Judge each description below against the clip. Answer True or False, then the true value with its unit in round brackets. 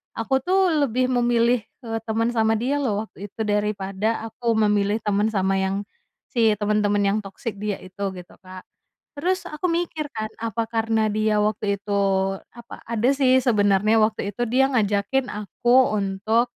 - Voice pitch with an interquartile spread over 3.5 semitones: False (2.9 semitones)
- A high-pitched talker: True (220 Hz)